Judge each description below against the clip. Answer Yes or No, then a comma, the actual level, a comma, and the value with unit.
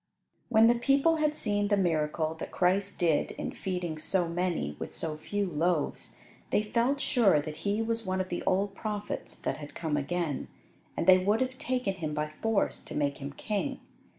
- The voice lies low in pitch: No, high, 190 Hz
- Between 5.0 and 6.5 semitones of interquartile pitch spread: Yes, wide, 5.6 semitones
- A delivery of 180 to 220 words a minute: Yes, average, 190 wpm